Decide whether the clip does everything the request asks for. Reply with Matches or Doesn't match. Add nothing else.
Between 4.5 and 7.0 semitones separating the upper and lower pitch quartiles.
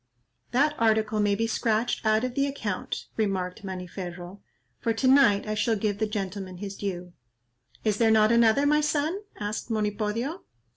Doesn't match